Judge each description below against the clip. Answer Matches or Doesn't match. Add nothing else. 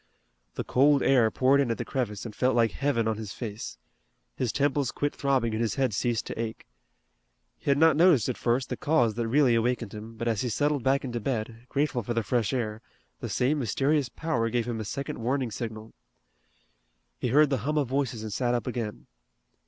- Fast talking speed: Matches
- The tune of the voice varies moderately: Matches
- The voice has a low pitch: Matches